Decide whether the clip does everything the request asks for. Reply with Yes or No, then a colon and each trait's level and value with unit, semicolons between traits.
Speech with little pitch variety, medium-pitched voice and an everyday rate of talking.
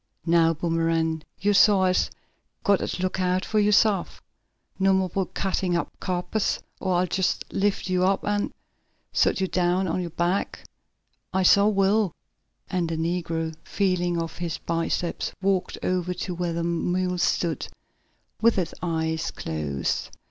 Yes: narrow, 2.3 semitones; medium, 180 Hz; average, 155 wpm